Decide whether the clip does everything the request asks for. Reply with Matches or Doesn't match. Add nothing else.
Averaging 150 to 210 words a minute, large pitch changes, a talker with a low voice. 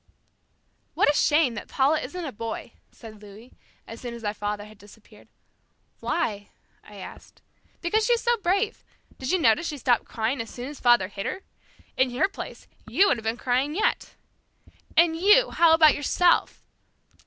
Doesn't match